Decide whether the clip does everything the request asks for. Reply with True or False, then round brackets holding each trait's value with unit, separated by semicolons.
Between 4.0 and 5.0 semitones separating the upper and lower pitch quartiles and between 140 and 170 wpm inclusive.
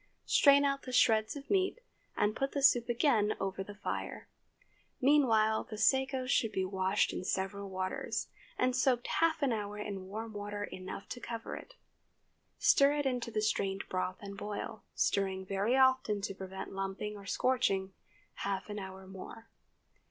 True (4.7 semitones; 160 wpm)